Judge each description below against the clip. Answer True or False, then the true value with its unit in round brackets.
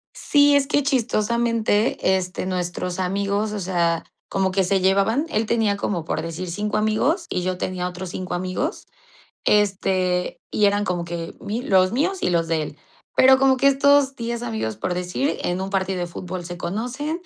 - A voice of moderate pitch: False (195 Hz)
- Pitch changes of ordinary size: True (4.6 semitones)